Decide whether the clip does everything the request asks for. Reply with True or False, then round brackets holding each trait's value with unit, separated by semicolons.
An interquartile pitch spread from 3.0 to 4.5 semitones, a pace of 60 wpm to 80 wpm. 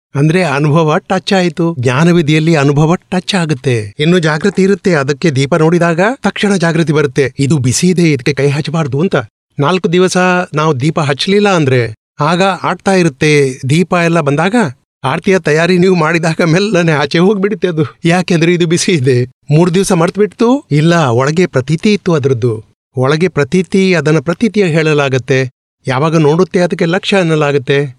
False (4.1 semitones; 140 wpm)